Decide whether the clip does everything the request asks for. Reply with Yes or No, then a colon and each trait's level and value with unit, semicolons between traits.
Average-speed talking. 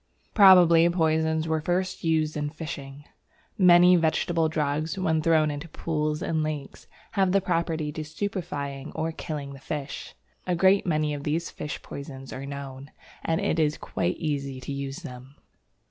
Yes: average, 160 wpm